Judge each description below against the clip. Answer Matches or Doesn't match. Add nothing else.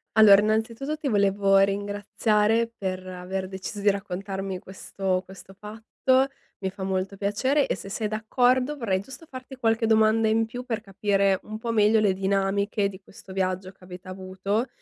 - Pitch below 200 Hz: Doesn't match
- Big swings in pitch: Doesn't match